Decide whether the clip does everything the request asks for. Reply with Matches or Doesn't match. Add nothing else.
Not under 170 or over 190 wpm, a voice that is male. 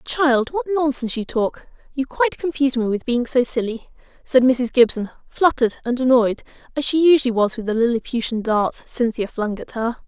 Doesn't match